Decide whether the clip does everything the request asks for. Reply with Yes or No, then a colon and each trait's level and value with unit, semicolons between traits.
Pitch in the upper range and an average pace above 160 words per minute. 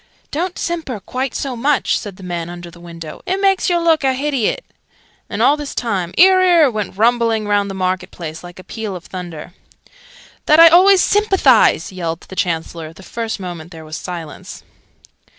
Yes: high, 210 Hz; average, 185 wpm